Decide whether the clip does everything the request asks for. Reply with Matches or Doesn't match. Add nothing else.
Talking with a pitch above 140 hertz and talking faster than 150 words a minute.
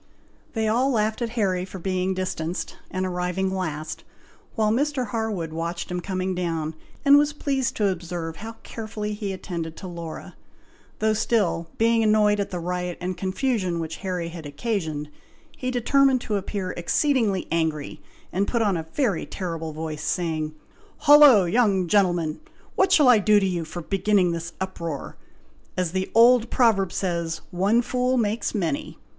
Matches